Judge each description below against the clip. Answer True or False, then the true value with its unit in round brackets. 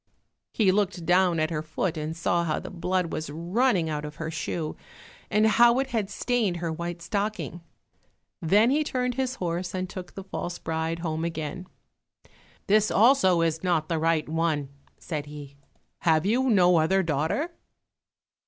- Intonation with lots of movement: False (4.2 semitones)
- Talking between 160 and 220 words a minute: True (165 wpm)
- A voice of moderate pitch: True (175 Hz)